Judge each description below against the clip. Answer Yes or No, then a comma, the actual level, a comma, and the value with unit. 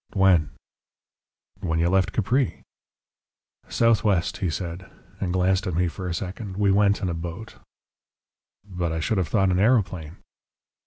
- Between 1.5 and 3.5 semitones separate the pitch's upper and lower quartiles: Yes, narrow, 2.6 semitones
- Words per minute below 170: Yes, average, 150 wpm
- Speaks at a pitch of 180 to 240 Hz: No, very low, 95 Hz